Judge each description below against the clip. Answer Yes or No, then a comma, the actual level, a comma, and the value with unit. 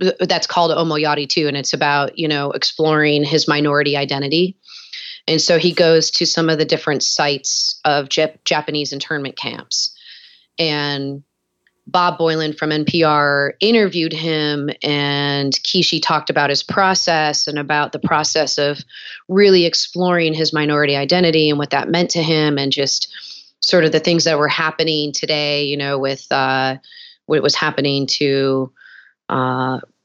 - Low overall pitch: No, medium, 150 Hz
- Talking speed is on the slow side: No, average, 150 wpm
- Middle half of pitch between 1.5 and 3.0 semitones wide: Yes, narrow, 2.4 semitones